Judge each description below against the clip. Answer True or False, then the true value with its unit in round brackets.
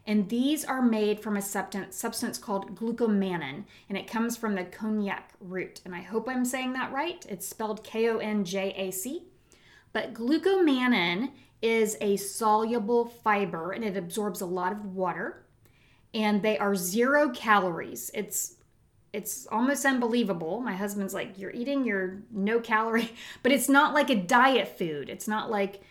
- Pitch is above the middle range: True (215 Hz)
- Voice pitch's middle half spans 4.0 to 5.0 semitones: False (3.5 semitones)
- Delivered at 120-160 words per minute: True (155 wpm)